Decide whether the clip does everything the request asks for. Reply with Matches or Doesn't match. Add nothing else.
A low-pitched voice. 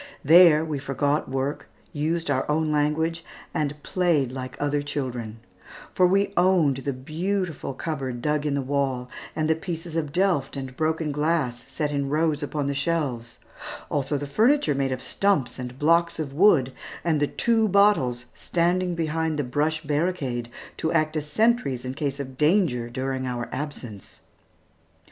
Doesn't match